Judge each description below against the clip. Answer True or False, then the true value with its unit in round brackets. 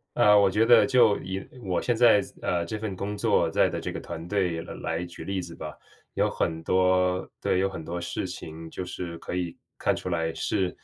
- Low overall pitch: True (90 Hz)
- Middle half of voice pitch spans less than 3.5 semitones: True (3.0 semitones)